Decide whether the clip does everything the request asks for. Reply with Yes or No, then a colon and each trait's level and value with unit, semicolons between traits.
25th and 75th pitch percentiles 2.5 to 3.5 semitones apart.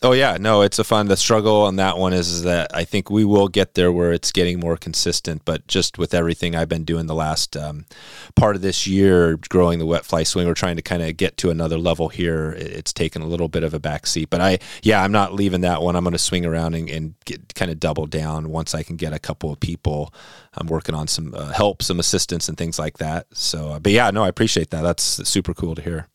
Yes: average, 2.9 semitones